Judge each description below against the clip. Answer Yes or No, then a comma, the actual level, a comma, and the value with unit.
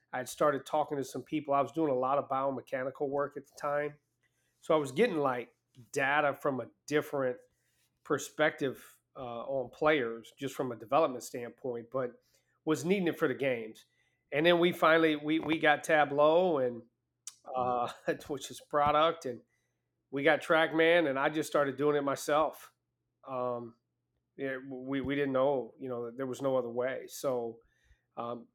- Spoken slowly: No, average, 175 wpm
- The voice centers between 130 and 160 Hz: Yes, medium, 140 Hz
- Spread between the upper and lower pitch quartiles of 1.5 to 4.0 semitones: Yes, average, 3.3 semitones